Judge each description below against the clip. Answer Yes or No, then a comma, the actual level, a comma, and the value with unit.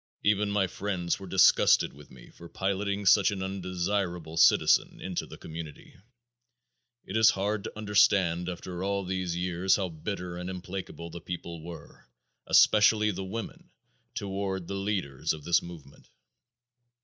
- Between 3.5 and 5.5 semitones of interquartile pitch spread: No, narrow, 2.5 semitones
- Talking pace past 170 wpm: No, average, 145 wpm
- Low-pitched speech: Yes, very low, 95 Hz